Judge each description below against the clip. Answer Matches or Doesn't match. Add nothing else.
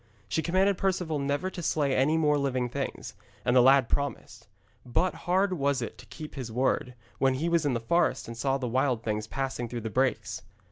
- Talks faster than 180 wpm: Matches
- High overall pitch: Doesn't match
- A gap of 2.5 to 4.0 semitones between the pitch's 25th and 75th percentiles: Doesn't match